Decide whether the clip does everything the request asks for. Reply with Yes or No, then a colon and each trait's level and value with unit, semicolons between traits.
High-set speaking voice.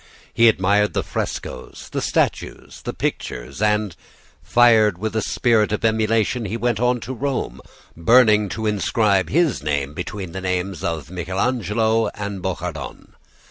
No: low, 105 Hz